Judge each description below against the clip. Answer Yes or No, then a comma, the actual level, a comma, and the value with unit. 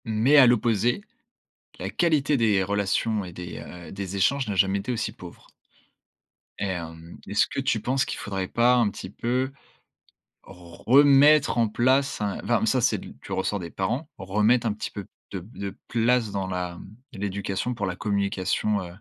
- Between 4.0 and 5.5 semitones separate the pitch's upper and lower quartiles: Yes, average, 4.3 semitones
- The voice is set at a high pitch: No, low, 105 Hz